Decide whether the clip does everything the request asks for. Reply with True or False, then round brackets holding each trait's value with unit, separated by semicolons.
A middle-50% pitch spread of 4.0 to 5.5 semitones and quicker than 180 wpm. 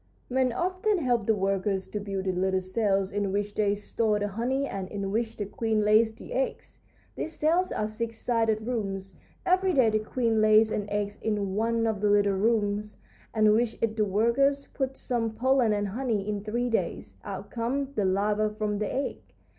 False (2.7 semitones; 195 wpm)